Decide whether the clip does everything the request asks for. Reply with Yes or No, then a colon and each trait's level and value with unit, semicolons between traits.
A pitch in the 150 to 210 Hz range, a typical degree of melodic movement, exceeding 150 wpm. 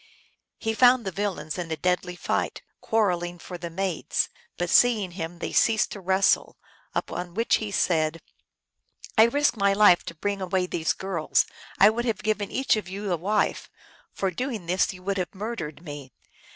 Yes: high, 190 Hz; average, 3.5 semitones; average, 185 wpm